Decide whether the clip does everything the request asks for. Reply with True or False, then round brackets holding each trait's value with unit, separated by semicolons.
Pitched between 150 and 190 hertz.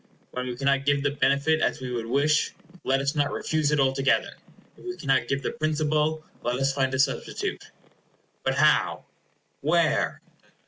False (140 Hz)